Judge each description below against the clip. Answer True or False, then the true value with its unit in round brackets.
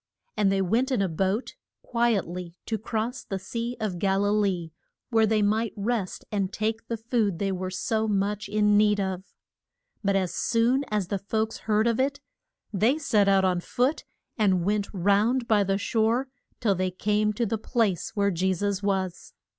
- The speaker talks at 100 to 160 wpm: False (185 wpm)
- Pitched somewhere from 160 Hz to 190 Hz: False (205 Hz)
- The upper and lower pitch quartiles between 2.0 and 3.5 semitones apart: True (2.6 semitones)